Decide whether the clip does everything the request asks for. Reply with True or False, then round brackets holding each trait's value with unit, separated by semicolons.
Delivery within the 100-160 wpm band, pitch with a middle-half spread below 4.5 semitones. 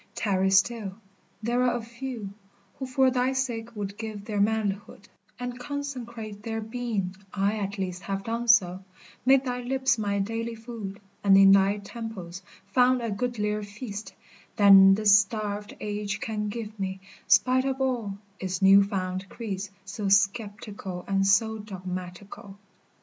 True (150 wpm; 3.1 semitones)